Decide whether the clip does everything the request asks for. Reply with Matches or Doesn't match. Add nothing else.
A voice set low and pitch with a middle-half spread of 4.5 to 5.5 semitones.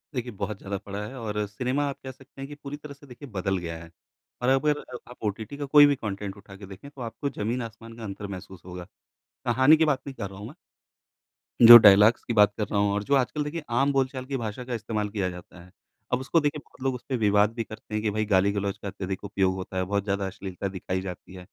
Matches